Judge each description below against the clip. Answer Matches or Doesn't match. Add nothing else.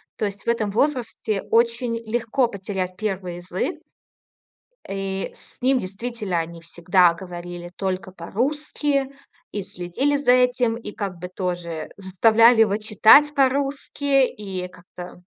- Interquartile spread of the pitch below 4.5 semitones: Doesn't match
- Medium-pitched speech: Doesn't match